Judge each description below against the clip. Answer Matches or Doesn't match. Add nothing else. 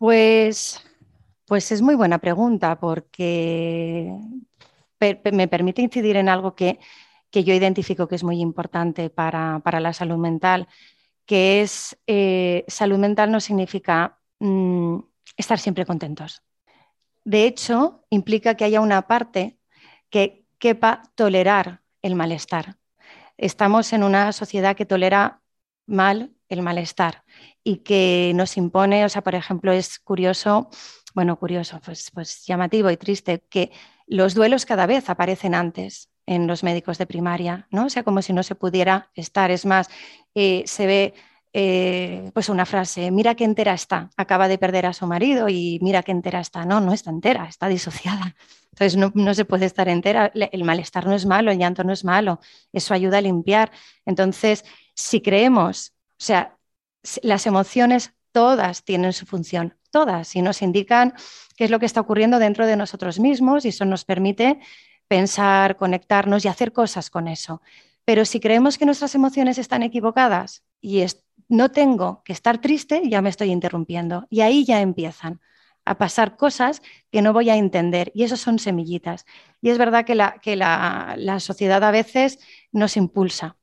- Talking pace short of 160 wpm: Doesn't match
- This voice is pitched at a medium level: Doesn't match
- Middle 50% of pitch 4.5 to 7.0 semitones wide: Doesn't match